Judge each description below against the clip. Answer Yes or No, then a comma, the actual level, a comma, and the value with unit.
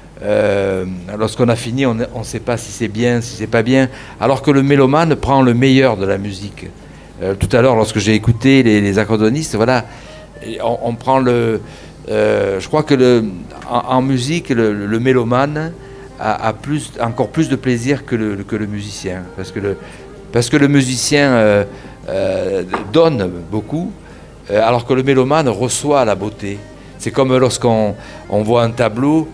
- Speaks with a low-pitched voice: Yes, low, 120 Hz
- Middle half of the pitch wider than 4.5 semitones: No, average, 3.8 semitones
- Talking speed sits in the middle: No, fast, 180 wpm